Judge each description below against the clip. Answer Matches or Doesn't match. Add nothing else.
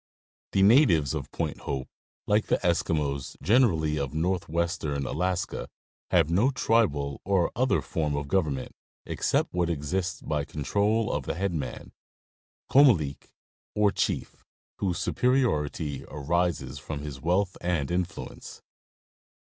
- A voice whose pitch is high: Doesn't match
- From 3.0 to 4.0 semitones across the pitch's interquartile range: Doesn't match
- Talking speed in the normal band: Doesn't match